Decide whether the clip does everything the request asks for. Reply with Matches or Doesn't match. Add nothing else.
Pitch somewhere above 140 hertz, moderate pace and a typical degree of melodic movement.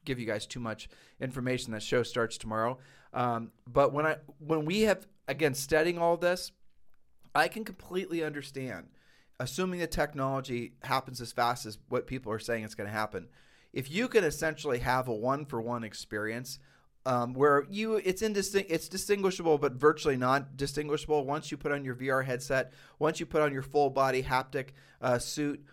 Doesn't match